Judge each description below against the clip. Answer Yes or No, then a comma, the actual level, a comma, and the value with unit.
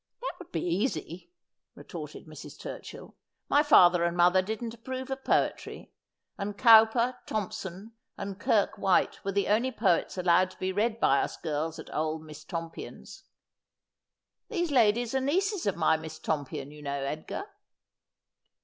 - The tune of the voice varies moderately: No, wide, 6.1 semitones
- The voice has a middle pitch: No, high, 195 Hz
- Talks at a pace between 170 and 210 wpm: No, average, 160 wpm